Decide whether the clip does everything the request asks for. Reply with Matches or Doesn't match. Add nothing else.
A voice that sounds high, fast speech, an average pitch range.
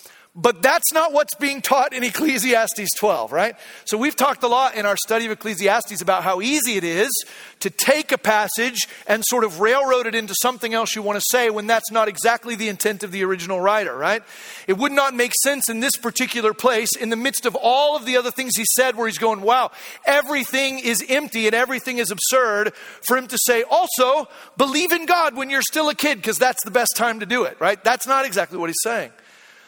Matches